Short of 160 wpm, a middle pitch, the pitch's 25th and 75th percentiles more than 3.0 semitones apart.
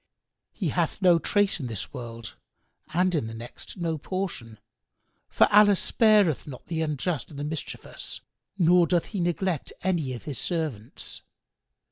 Yes: average, 150 wpm; medium, 165 Hz; wide, 5.6 semitones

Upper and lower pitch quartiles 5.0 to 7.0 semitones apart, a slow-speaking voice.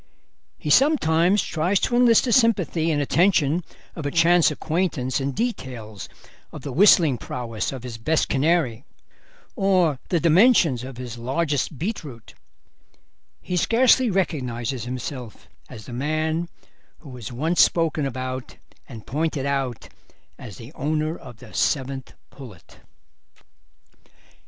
Yes: average, 5.3 semitones; slow, 125 wpm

